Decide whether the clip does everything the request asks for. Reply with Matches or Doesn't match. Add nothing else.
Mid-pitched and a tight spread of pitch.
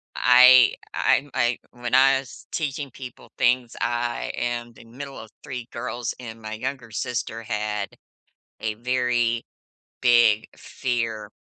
Doesn't match